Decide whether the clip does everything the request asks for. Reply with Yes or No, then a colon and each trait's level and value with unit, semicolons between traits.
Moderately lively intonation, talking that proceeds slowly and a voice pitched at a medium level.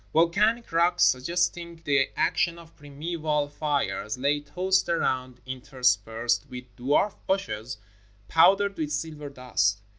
Yes: average, 5.0 semitones; slow, 120 wpm; medium, 150 Hz